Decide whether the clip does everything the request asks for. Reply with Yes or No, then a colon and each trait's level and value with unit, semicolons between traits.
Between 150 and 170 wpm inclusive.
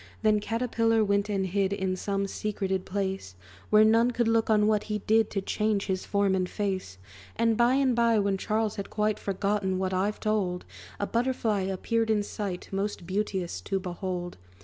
No: average, 180 wpm